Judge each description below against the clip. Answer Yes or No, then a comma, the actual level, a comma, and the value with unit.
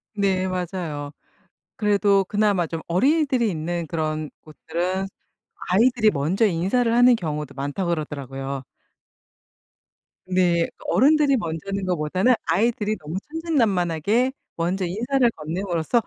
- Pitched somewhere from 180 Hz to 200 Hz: Yes, medium, 185 Hz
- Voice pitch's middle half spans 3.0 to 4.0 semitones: No, wide, 5.5 semitones